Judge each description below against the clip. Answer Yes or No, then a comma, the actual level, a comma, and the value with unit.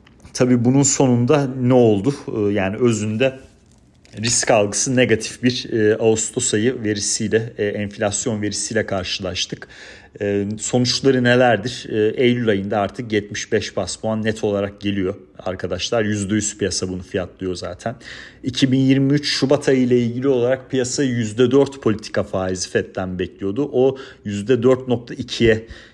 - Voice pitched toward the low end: Yes, low, 110 Hz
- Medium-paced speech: Yes, average, 110 wpm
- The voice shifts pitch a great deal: No, average, 3.8 semitones